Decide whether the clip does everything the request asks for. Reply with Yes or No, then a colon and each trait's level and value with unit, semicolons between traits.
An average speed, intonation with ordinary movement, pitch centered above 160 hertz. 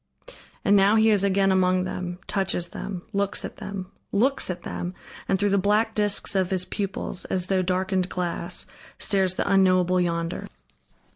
No: average, 165 wpm; narrow, 1.6 semitones; high, 190 Hz